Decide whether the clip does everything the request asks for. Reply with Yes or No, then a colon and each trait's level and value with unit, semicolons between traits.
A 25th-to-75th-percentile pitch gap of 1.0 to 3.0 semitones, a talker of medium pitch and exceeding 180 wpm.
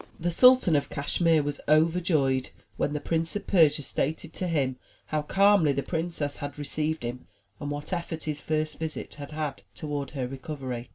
No: narrow, 2.4 semitones; medium, 150 Hz; average, 175 wpm